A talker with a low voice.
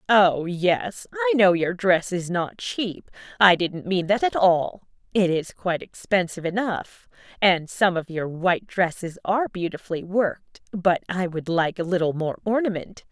No: medium, 185 Hz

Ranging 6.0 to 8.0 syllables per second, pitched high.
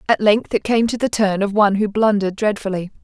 Yes: 6.1 syllables/s; high, 205 Hz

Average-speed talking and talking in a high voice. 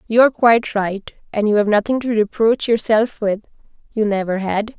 Yes: average, 150 wpm; high, 215 Hz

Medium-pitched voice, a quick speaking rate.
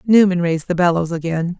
No: medium, 175 Hz; average, 190 wpm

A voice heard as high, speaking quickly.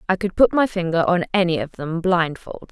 No: medium, 180 Hz; fast, 245 wpm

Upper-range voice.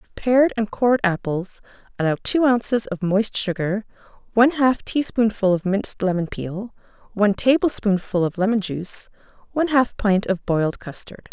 Yes: high, 210 Hz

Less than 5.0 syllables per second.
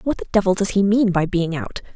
No: 5.8 syllables/s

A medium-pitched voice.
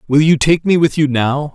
Yes: medium, 145 Hz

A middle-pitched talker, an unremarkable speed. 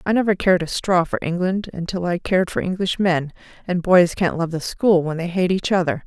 No: medium, 175 Hz; fast, 230 wpm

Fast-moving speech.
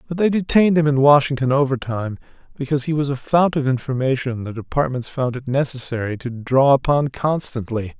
No: average, 175 wpm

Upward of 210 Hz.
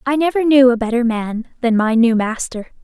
Yes: high, 245 Hz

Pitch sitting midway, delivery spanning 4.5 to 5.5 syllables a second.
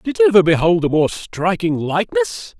Yes: medium, 160 Hz; 5.1 syllables/s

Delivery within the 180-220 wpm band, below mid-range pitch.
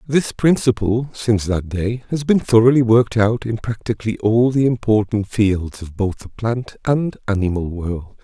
No: average, 170 wpm; low, 110 Hz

